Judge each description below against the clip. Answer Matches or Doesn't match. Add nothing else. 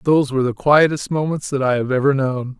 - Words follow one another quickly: Matches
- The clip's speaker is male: Matches